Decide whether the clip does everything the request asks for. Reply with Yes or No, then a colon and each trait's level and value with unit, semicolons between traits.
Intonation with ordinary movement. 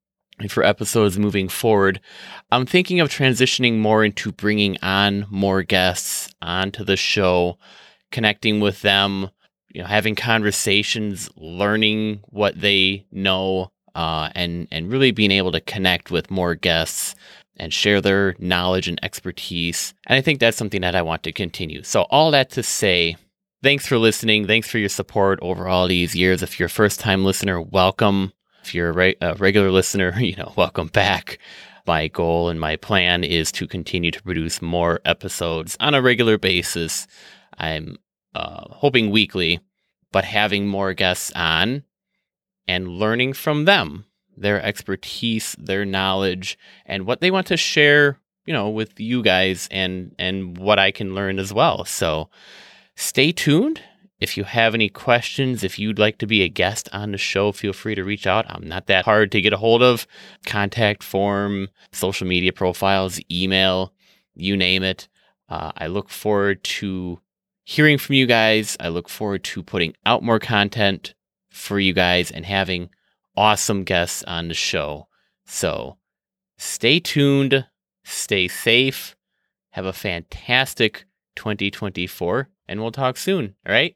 Yes: average, 3.3 semitones